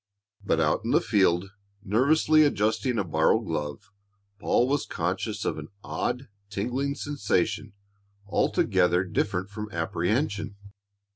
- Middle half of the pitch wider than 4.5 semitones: Yes, wide, 5.4 semitones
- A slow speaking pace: Yes, slow, 120 wpm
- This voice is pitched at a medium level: No, low, 100 Hz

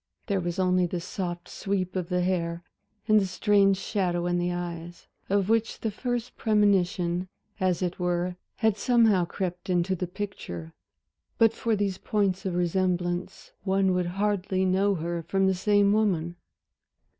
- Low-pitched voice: No, medium, 185 Hz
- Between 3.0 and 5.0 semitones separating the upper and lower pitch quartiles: No, narrow, 2.4 semitones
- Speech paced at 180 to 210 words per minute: No, average, 155 wpm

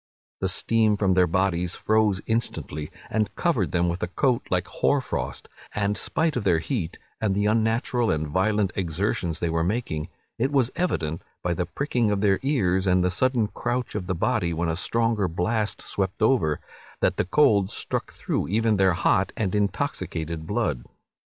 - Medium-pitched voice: No, low, 100 Hz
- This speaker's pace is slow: No, average, 175 wpm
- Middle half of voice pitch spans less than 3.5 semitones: No, average, 4.2 semitones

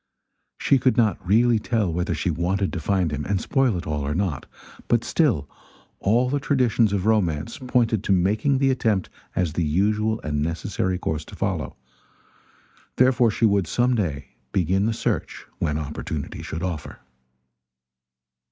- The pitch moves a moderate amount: No, wide, 5.7 semitones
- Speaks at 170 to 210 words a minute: No, average, 160 wpm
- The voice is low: Yes, low, 100 Hz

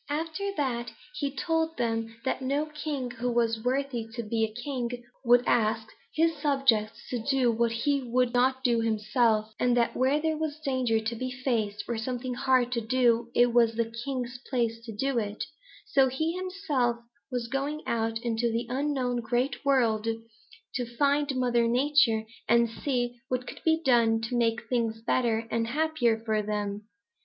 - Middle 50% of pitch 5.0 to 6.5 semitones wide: No, average, 3.1 semitones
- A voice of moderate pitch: No, high, 245 Hz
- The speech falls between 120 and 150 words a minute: No, average, 170 wpm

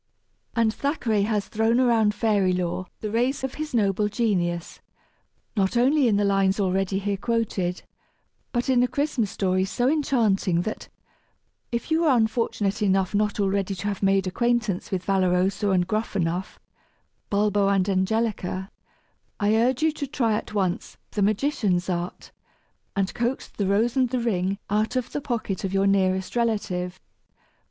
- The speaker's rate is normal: Yes, average, 155 wpm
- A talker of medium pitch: No, high, 205 Hz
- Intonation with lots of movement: No, average, 3.5 semitones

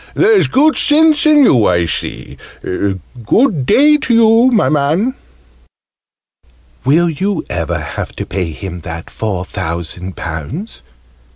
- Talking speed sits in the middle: No, slow, 125 wpm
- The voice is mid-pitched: Yes, medium, 145 Hz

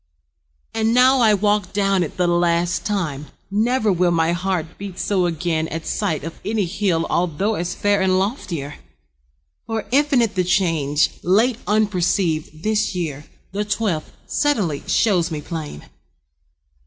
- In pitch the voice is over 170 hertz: Yes, medium, 185 Hz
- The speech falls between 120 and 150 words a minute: Yes, average, 140 wpm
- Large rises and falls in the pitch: No, average, 4.2 semitones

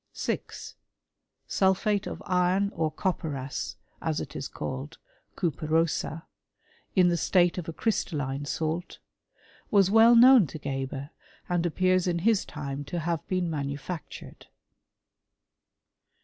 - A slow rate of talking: Yes, slow, 120 wpm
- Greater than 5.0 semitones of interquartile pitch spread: No, average, 3.8 semitones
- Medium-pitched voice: Yes, medium, 170 Hz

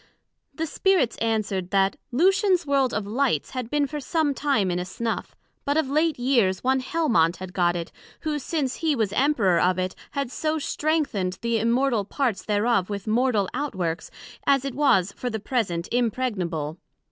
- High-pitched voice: Yes, high, 240 Hz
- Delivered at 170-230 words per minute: Yes, average, 175 wpm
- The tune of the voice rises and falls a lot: Yes, wide, 6.6 semitones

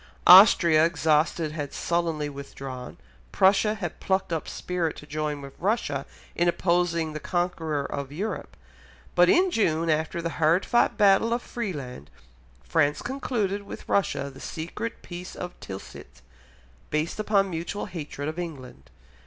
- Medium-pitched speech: Yes, medium, 165 Hz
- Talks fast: No, average, 140 wpm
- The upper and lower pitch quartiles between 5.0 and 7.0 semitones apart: No, average, 4.4 semitones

